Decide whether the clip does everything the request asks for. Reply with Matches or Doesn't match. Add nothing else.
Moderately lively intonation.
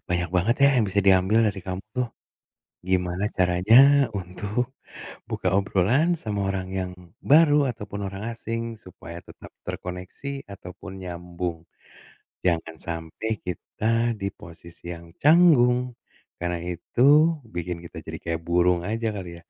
Matches